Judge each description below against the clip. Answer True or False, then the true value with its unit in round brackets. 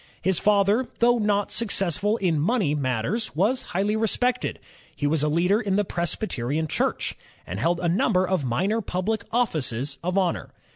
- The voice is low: False (190 Hz)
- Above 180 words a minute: False (165 wpm)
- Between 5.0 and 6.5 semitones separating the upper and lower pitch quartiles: True (5.3 semitones)